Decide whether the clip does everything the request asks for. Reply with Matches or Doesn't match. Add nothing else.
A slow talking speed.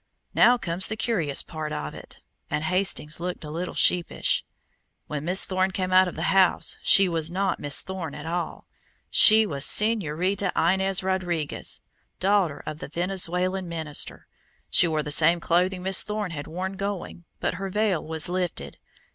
Doesn't match